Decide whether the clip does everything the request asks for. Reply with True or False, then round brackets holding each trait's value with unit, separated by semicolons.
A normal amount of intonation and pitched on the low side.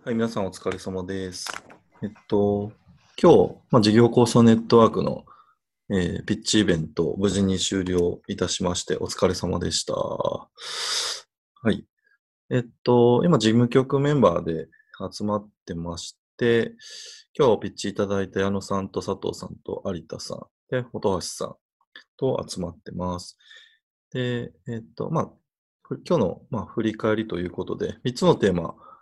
True (4.5 semitones; 110 Hz)